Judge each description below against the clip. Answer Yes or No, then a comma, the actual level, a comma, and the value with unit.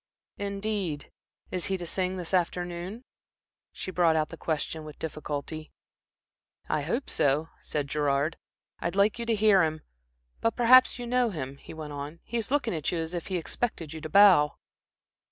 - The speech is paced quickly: No, average, 175 wpm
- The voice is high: No, medium, 170 Hz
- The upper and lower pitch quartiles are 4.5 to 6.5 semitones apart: Yes, average, 4.8 semitones